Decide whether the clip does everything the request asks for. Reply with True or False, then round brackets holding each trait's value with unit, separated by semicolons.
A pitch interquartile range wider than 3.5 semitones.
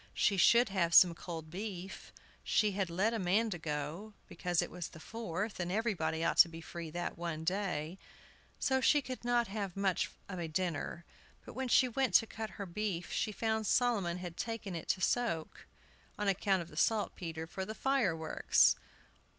True (4.5 semitones)